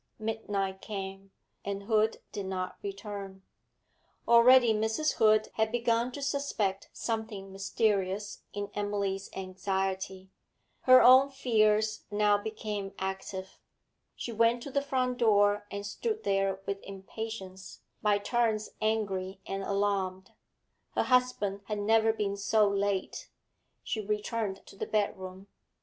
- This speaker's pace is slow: Yes, slow, 125 wpm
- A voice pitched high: Yes, high, 205 Hz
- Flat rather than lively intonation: Yes, narrow, 2.3 semitones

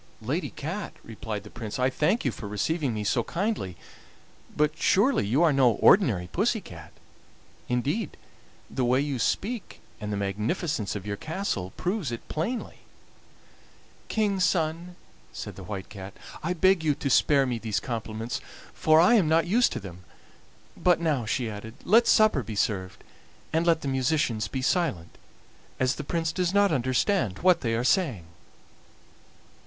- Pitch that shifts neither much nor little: No, wide, 8.2 semitones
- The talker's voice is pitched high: No, medium, 140 Hz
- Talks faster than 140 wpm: Yes, average, 160 wpm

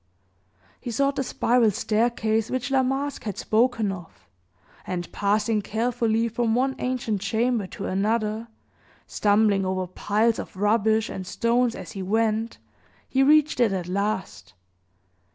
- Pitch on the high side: Yes, high, 220 Hz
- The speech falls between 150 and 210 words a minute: No, slow, 135 wpm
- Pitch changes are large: No, average, 3.2 semitones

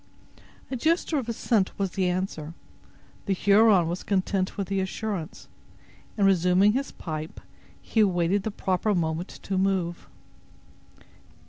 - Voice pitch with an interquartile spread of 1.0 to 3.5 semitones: Yes, narrow, 2.6 semitones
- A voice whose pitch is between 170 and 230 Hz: Yes, high, 190 Hz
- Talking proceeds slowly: Yes, slow, 130 wpm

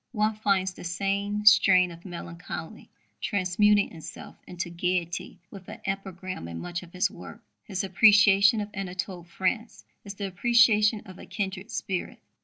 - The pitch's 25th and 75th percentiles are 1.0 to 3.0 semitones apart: Yes, narrow, 2.6 semitones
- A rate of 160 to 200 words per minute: No, average, 150 wpm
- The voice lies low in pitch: No, high, 195 Hz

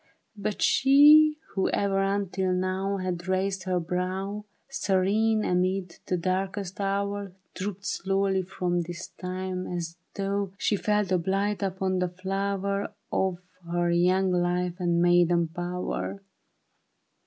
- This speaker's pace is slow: Yes, slow, 125 wpm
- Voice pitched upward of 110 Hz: Yes, high, 190 Hz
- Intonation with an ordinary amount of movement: No, narrow, 1.7 semitones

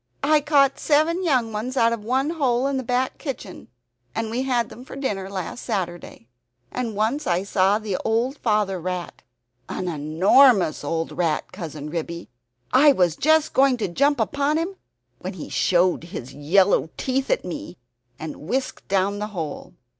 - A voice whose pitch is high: Yes, high, 220 Hz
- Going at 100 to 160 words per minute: No, average, 170 wpm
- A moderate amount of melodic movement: No, wide, 6.9 semitones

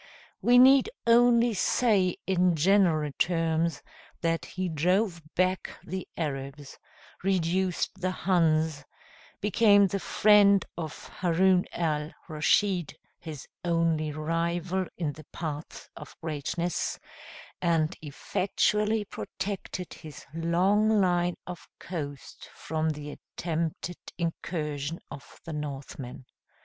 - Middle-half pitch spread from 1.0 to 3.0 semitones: No, average, 3.4 semitones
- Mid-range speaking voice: Yes, medium, 170 Hz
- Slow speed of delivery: Yes, slow, 105 wpm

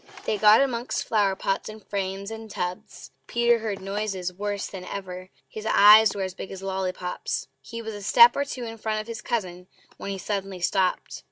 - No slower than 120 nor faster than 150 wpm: No, average, 200 wpm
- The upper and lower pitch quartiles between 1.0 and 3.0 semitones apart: Yes, narrow, 2.5 semitones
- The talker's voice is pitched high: Yes, high, 200 Hz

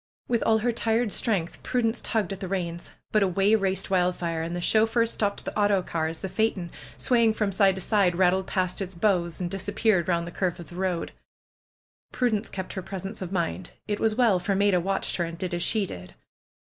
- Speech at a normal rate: No, fast, 210 wpm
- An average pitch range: Yes, average, 3.4 semitones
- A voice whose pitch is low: No, high, 190 Hz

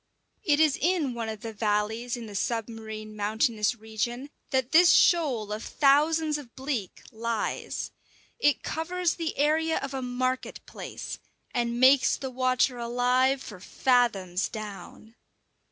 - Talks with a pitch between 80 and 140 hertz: No, high, 245 Hz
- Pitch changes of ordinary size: Yes, average, 4.2 semitones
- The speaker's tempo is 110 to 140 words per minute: Yes, slow, 135 wpm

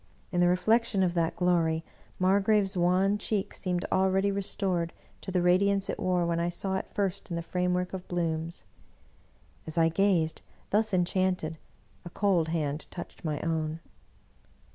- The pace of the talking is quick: No, average, 165 wpm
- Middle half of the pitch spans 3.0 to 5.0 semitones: No, narrow, 2.4 semitones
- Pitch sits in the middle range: Yes, medium, 180 Hz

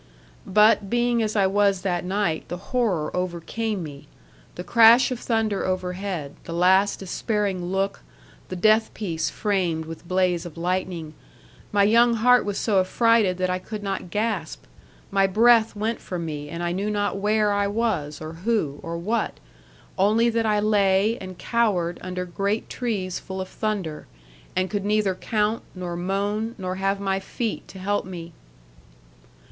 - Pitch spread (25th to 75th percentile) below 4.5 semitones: Yes, average, 3.1 semitones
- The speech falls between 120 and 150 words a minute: No, average, 165 wpm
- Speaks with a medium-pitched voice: No, high, 195 Hz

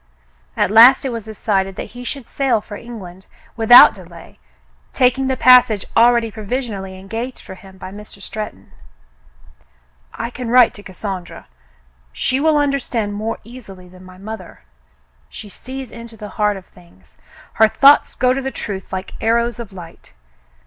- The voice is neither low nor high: No, high, 220 Hz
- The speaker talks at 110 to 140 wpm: No, average, 155 wpm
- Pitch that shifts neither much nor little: Yes, average, 4.3 semitones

